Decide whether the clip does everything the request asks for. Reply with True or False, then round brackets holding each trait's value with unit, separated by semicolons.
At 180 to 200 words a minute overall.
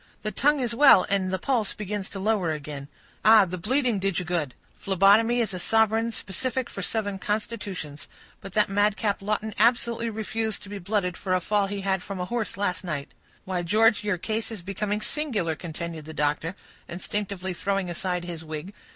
True (185 wpm)